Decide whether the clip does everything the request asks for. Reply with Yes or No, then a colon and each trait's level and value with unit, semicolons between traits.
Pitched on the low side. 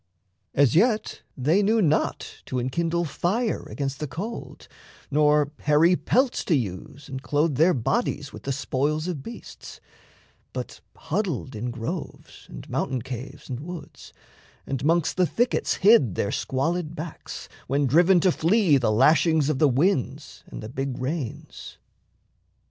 No: medium, 150 Hz